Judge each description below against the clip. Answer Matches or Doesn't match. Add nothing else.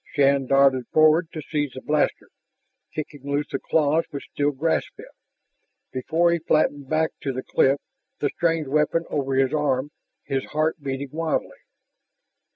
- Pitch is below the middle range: Doesn't match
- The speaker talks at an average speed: Matches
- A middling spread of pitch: Doesn't match